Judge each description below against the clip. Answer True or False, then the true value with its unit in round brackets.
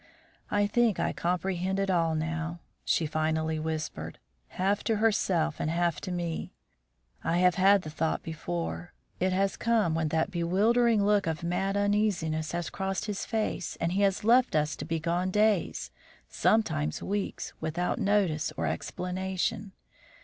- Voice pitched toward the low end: False (180 Hz)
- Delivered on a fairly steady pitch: False (4.0 semitones)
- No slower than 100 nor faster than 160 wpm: True (155 wpm)